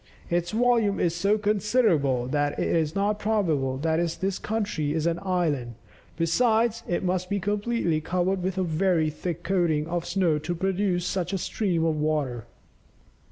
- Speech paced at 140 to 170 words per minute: Yes, average, 160 wpm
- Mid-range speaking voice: Yes, medium, 175 Hz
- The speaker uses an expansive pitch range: No, average, 4.2 semitones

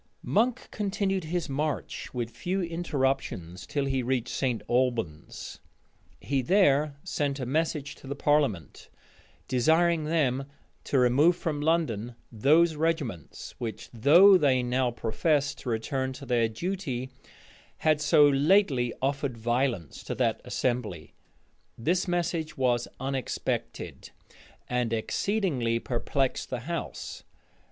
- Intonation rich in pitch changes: No, average, 4.7 semitones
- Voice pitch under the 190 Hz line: Yes, low, 135 Hz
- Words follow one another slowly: Yes, slow, 120 wpm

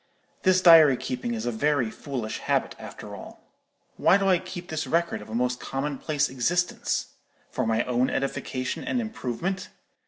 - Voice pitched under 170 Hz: Yes, medium, 140 Hz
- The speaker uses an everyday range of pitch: No, wide, 5.9 semitones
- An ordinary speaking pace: Yes, average, 160 wpm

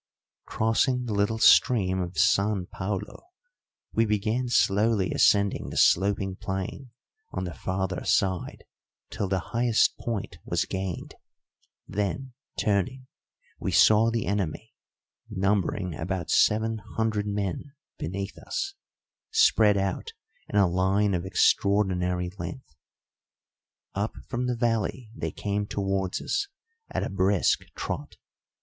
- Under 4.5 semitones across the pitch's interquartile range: Yes, average, 2.9 semitones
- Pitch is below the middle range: Yes, low, 100 Hz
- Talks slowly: Yes, slow, 120 wpm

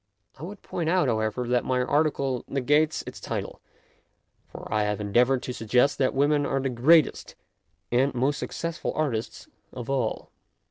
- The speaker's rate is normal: Yes, average, 165 wpm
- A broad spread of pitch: No, average, 3.4 semitones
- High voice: No, low, 135 Hz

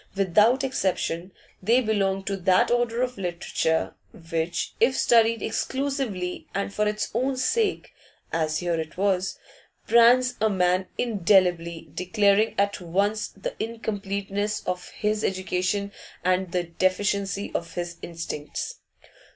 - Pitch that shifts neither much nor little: Yes, average, 3.7 semitones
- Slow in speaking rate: Yes, slow, 125 wpm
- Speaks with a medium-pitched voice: No, high, 200 Hz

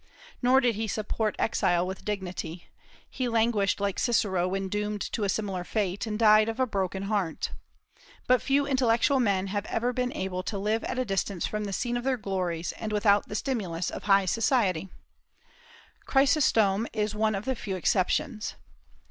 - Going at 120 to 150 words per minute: No, average, 175 wpm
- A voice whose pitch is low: No, high, 210 Hz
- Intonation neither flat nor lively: Yes, average, 3.3 semitones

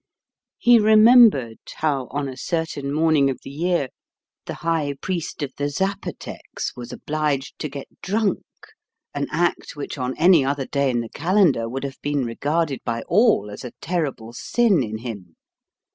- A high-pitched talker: No, medium, 145 Hz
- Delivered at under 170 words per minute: Yes, average, 160 wpm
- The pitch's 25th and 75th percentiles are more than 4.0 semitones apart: Yes, average, 4.7 semitones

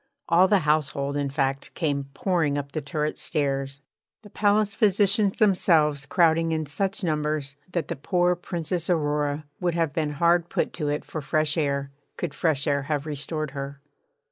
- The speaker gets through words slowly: No, average, 170 wpm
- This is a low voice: No, medium, 155 Hz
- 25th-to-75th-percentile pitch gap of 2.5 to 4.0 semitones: Yes, average, 3.4 semitones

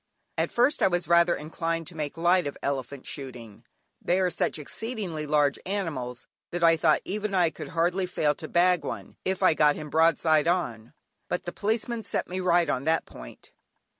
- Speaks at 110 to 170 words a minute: No, average, 190 wpm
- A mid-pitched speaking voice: Yes, medium, 165 Hz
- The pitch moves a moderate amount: Yes, average, 3.6 semitones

